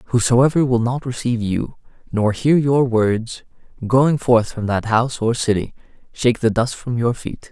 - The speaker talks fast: No, average, 175 wpm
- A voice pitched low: Yes, low, 120 Hz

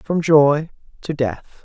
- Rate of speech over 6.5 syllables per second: No, 3.3 syllables/s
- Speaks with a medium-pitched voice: Yes, medium, 150 Hz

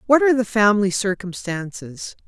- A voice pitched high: Yes, high, 210 Hz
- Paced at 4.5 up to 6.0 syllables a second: Yes, 5.4 syllables/s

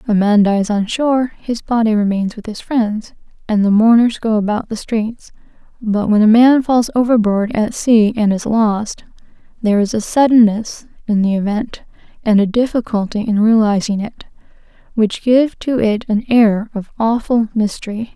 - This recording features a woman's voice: Yes, female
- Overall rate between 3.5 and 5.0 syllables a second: Yes, 4.7 syllables/s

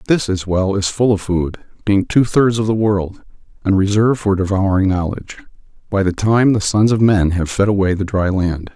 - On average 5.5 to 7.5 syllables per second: No, 5.1 syllables/s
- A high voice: No, low, 100 Hz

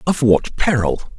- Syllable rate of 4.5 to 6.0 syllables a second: No, 3.9 syllables/s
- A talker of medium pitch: No, low, 130 Hz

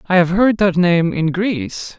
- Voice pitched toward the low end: No, medium, 180 Hz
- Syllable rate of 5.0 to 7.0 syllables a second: No, 4.3 syllables/s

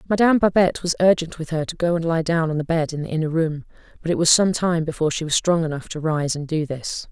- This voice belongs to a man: No, female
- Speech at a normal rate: No, fast, 280 wpm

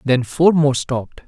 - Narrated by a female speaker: No, male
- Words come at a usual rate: Yes, average, 190 wpm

